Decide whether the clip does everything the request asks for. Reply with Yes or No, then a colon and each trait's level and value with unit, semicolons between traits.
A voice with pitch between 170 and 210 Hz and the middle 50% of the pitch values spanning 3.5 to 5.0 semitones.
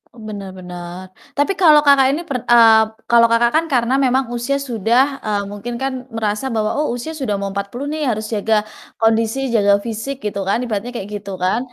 No: high, 230 Hz; average, 4.2 semitones